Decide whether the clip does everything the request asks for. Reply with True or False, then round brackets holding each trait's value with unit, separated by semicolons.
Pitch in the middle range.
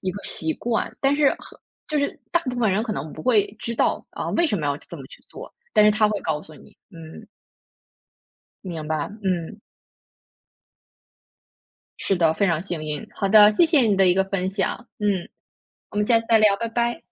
False (200 Hz)